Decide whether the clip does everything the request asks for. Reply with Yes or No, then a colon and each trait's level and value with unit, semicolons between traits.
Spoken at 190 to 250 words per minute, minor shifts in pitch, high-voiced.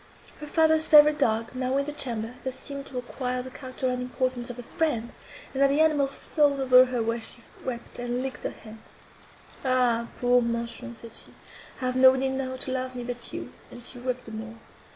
Yes: fast, 205 wpm; narrow, 1.9 semitones; very high, 255 Hz